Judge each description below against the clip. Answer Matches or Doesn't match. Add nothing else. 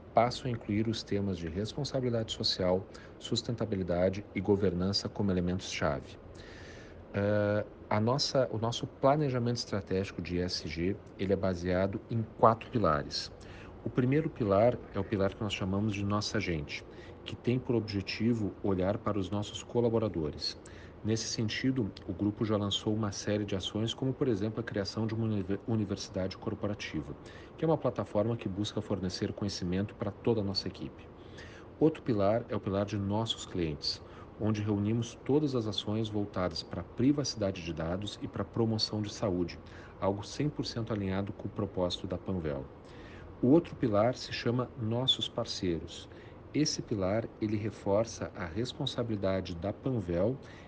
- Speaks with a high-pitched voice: Doesn't match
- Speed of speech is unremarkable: Matches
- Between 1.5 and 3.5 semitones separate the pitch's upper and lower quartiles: Matches